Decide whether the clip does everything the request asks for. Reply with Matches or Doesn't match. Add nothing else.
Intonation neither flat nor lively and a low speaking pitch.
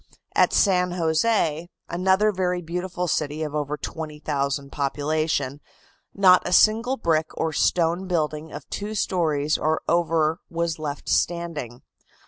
Doesn't match